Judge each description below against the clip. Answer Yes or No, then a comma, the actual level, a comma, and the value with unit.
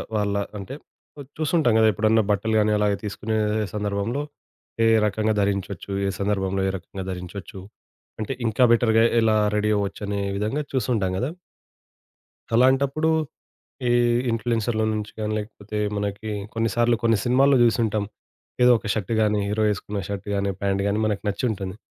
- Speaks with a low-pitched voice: Yes, low, 105 Hz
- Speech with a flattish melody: Yes, narrow, 2.3 semitones